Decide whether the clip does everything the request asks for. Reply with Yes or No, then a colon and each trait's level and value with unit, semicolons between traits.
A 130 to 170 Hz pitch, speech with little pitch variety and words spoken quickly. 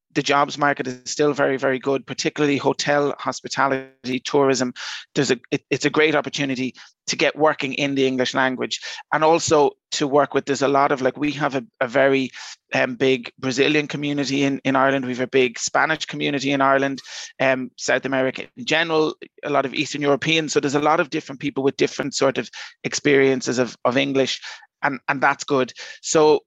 Yes: medium, 140 Hz; narrow, 1.8 semitones; fast, 195 wpm